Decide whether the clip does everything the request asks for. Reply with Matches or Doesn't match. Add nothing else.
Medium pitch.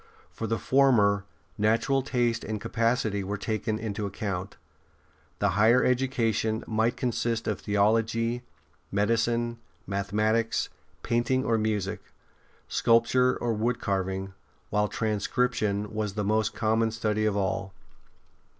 Doesn't match